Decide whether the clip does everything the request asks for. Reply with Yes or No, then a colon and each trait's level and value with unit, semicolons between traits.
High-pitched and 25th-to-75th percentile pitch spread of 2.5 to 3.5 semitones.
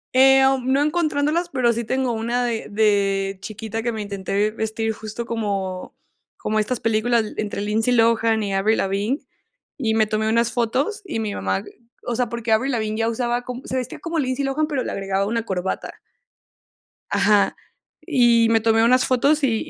Yes: high, 225 Hz; average, 3.0 semitones